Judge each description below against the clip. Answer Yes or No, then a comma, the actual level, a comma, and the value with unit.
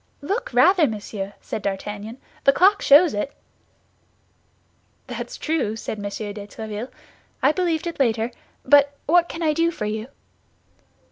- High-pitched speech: Yes, very high, 270 Hz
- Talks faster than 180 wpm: No, average, 140 wpm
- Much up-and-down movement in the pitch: Yes, wide, 7.6 semitones